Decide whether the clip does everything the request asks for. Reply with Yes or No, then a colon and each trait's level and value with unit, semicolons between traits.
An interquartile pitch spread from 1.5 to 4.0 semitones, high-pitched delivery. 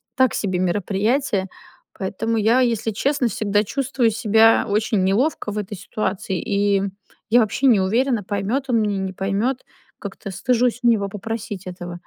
Yes: average, 3.3 semitones; high, 215 Hz